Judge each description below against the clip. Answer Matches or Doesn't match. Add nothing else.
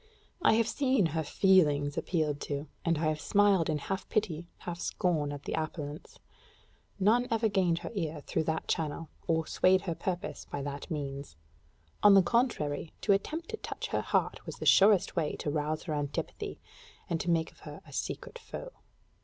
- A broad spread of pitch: Doesn't match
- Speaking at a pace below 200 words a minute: Matches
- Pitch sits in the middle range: Matches